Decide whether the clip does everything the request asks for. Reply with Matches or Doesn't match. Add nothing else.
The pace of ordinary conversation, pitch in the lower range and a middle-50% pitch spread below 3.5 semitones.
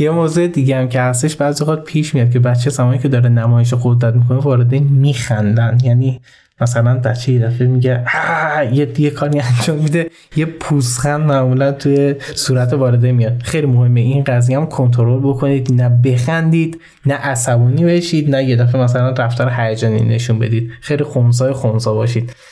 Doesn't match